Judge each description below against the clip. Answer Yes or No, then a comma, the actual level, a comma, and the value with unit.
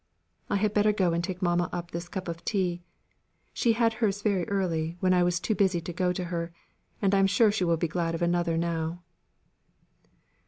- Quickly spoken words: Yes, fast, 210 wpm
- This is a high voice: No, medium, 180 Hz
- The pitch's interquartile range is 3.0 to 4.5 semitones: No, narrow, 2.5 semitones